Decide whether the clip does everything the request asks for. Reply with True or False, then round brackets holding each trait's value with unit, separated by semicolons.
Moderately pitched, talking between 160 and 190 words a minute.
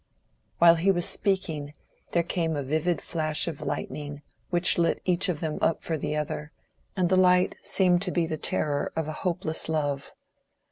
True (165 Hz; 175 wpm)